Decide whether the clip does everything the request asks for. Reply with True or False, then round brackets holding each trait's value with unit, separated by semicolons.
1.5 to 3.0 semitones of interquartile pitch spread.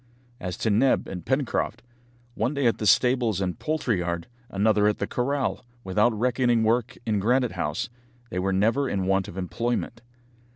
False (4.3 semitones)